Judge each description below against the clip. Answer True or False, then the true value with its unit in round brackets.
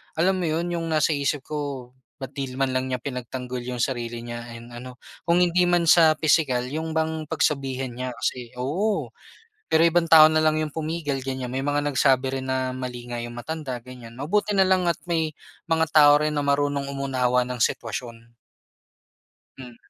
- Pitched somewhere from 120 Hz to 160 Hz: True (140 Hz)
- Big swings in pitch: False (4.0 semitones)